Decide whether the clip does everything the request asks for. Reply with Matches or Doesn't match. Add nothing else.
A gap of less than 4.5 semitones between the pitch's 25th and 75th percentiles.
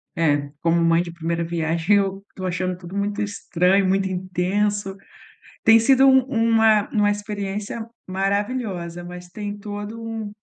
Matches